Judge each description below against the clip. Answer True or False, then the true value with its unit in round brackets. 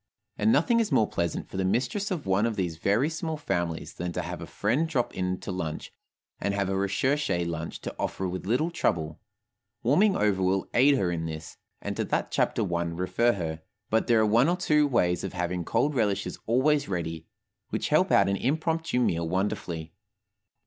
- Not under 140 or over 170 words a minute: False (195 wpm)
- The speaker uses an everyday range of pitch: False (7.4 semitones)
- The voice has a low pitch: True (100 Hz)